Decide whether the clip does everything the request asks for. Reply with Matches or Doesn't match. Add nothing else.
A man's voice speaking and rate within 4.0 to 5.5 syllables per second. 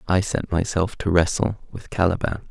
Matches